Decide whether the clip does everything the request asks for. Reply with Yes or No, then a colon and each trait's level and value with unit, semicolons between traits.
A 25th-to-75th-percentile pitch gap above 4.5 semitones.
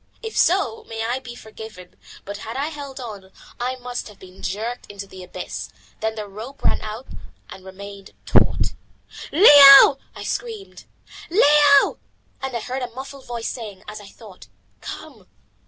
Yes: average, 5.0 semitones